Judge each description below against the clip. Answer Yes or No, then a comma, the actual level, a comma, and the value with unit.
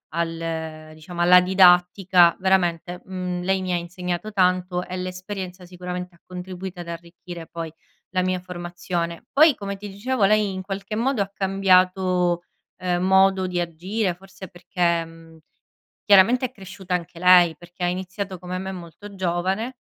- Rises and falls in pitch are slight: Yes, narrow, 1.6 semitones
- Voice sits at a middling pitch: Yes, medium, 180 Hz